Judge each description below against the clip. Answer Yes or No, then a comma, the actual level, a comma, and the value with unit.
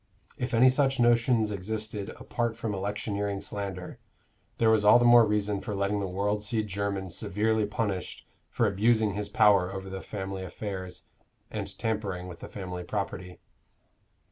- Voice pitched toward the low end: Yes, low, 105 Hz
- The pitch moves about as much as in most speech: No, narrow, 2.3 semitones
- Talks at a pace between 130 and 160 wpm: Yes, average, 155 wpm